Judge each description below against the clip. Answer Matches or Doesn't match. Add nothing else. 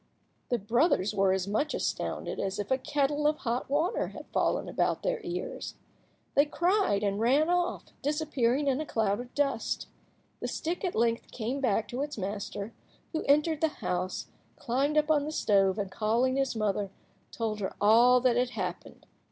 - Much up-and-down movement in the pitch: Matches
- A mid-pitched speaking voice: Doesn't match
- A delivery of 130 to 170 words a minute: Doesn't match